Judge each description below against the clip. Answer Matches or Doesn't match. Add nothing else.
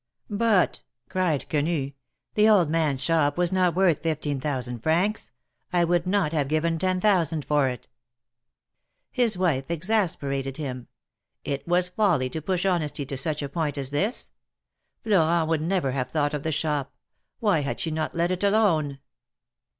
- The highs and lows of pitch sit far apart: Doesn't match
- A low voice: Doesn't match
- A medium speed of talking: Matches